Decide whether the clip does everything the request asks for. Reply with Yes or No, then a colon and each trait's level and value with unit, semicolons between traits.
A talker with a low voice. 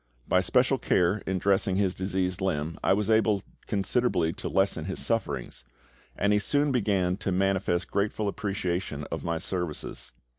Yes: very low, 95 Hz